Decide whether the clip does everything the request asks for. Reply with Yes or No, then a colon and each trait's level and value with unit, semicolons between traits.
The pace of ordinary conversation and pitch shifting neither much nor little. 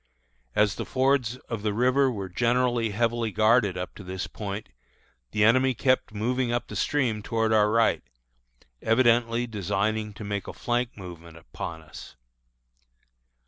Yes: average, 145 wpm; average, 3.0 semitones